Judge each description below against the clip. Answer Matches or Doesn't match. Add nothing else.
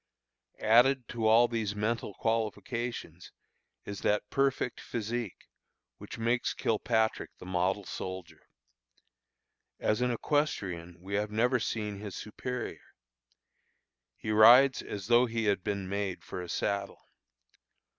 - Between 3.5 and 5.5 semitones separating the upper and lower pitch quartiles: Doesn't match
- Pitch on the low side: Matches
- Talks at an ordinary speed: Doesn't match